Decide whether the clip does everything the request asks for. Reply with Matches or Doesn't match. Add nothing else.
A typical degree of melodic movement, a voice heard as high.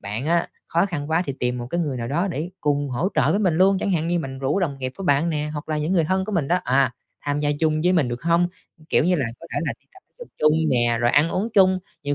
Doesn't match